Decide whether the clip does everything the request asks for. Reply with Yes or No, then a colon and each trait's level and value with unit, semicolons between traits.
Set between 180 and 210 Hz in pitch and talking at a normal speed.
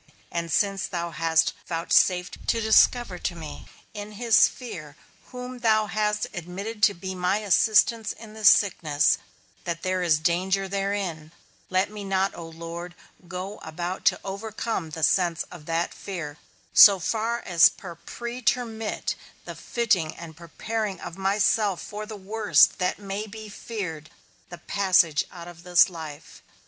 Yes: high, 190 Hz; average, 150 wpm